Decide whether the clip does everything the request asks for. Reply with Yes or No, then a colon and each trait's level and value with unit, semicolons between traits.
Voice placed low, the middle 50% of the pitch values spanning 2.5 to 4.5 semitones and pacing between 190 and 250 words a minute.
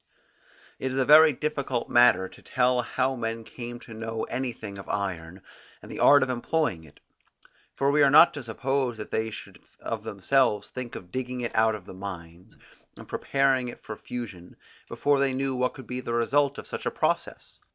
Yes: low, 125 Hz; average, 3.4 semitones; average, 195 wpm